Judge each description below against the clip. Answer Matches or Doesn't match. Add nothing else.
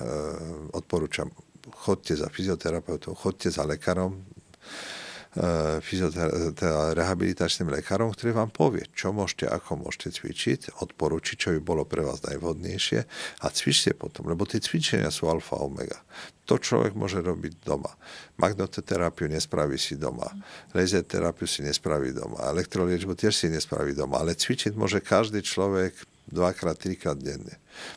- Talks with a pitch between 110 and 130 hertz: Doesn't match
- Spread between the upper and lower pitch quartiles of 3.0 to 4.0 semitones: Matches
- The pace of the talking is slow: Doesn't match